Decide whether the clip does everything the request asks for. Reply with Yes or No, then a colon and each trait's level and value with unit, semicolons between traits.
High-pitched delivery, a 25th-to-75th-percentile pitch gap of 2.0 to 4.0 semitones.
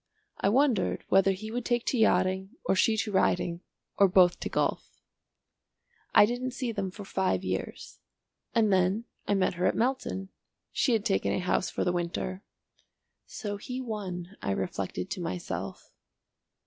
Yes: high, 195 Hz; average, 3.6 semitones